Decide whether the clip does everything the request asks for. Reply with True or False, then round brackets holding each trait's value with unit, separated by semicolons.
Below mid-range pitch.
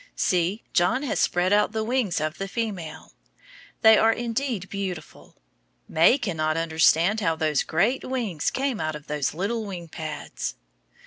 False (190 Hz)